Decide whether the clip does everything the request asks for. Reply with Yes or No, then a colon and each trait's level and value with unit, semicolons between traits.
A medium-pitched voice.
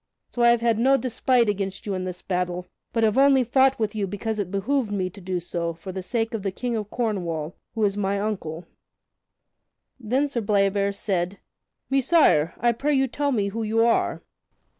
No: high, 210 Hz